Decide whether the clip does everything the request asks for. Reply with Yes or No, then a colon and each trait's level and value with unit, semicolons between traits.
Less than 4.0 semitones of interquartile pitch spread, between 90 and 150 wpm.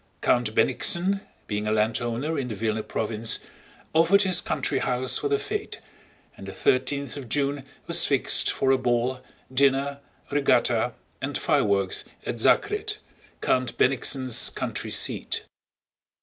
No: average, 5.2 semitones; slow, 135 wpm